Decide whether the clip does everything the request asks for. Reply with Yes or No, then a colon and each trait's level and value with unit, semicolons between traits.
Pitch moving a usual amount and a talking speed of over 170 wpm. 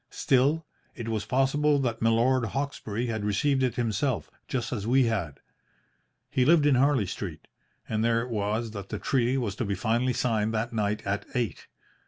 Yes: average, 3.5 semitones; average, 180 wpm